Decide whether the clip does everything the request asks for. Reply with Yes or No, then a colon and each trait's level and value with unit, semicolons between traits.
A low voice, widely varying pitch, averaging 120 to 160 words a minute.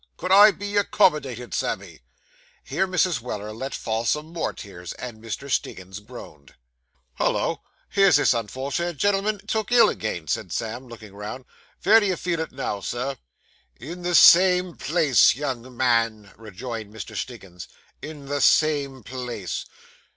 Yes: low, 130 Hz; wide, 7.7 semitones; average, 145 wpm